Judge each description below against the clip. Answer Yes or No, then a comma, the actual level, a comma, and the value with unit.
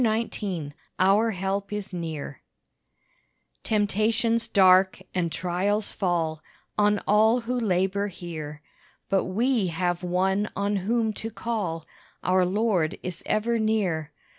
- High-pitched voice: Yes, high, 195 Hz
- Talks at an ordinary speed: No, slow, 115 wpm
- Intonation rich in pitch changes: No, average, 3.3 semitones